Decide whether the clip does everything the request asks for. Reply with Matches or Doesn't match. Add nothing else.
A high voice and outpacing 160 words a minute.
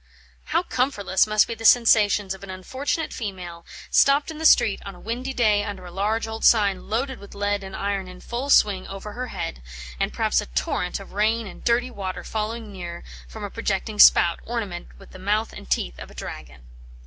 Matches